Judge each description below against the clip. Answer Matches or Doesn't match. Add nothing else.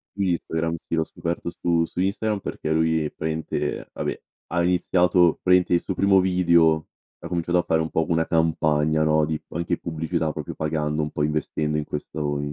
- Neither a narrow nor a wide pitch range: Doesn't match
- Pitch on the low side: Matches